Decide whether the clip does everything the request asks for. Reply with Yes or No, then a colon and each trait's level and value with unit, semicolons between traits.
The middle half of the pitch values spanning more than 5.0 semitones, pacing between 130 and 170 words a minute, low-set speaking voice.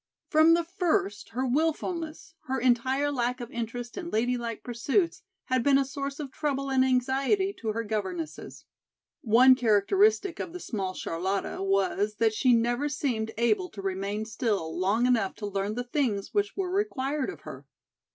No: wide, 5.4 semitones; average, 165 wpm; very high, 250 Hz